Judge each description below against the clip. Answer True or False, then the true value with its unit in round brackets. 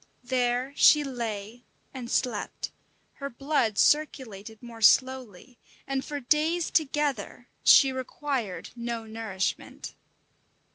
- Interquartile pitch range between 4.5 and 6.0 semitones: False (3.6 semitones)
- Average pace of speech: False (100 wpm)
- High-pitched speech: True (250 Hz)